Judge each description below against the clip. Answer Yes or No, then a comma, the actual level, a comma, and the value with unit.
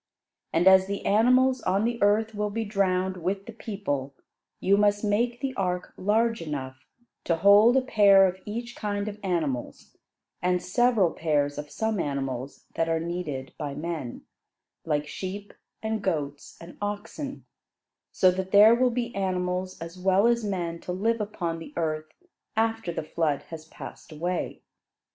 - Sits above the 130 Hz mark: Yes, high, 190 Hz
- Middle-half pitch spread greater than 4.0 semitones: Yes, average, 4.4 semitones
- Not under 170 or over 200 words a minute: No, average, 160 wpm